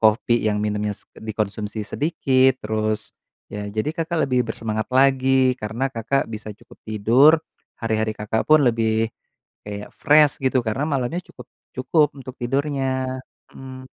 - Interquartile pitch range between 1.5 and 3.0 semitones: No, average, 3.6 semitones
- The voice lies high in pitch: No, low, 120 Hz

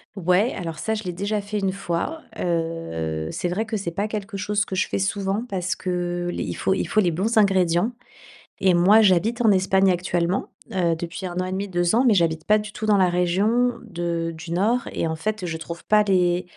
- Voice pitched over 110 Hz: Yes, medium, 185 Hz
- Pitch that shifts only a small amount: No, average, 3.2 semitones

